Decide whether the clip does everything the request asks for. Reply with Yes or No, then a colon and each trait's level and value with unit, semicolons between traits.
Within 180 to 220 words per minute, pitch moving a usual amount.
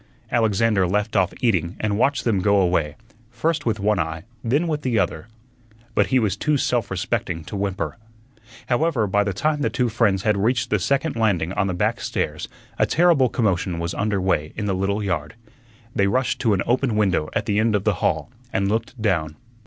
Yes: average, 200 wpm; average, 4.1 semitones